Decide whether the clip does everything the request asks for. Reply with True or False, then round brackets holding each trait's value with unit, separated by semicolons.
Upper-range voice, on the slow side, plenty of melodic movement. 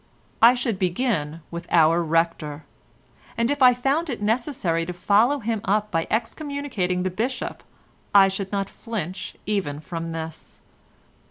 False (200 Hz; 145 wpm; 6.0 semitones)